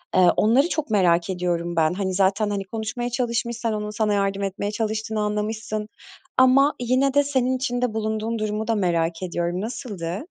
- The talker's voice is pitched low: No, high, 215 Hz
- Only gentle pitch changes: No, average, 3.8 semitones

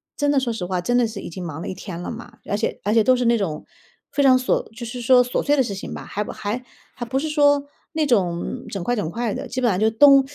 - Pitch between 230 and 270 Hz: Yes, high, 235 Hz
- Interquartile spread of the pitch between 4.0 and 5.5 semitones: Yes, average, 4.6 semitones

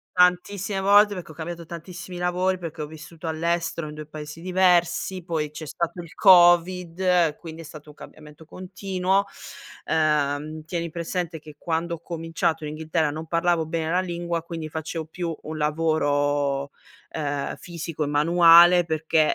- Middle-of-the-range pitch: Yes, medium, 165 Hz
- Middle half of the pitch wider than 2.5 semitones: No, narrow, 2.1 semitones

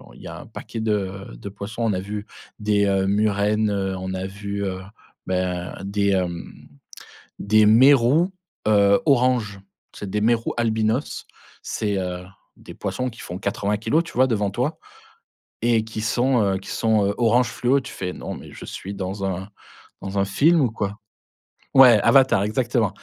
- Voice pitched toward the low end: Yes, low, 105 Hz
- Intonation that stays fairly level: No, average, 3.1 semitones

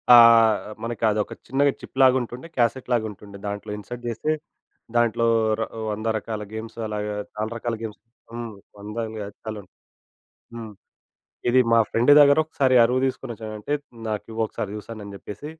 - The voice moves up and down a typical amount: No, narrow, 2.3 semitones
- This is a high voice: No, low, 115 Hz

